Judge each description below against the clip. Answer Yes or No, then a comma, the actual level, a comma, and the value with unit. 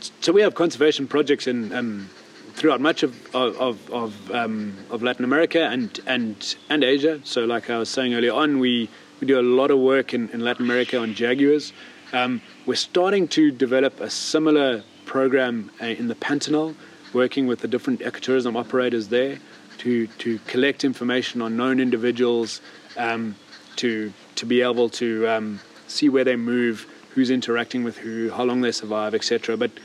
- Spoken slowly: No, average, 175 wpm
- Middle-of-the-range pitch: No, low, 125 Hz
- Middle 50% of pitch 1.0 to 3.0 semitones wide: Yes, narrow, 2.5 semitones